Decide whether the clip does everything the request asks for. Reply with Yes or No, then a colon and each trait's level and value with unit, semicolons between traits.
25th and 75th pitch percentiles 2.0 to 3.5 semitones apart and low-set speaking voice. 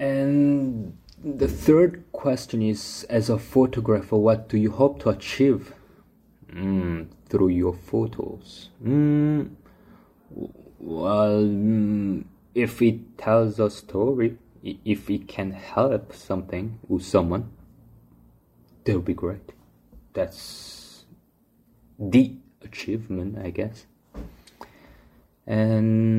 No: average, 4.1 semitones; low, 110 Hz